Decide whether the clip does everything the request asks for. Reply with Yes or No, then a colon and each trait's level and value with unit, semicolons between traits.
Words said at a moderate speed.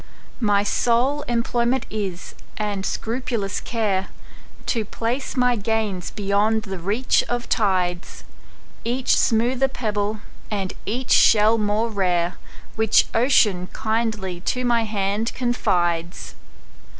No: slow, 100 wpm